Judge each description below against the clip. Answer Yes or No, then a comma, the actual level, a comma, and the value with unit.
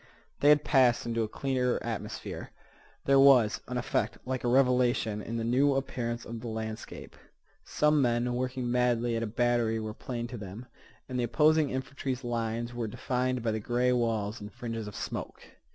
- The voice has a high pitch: No, low, 120 Hz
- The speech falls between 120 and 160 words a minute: No, average, 180 wpm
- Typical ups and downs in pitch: No, narrow, 2.0 semitones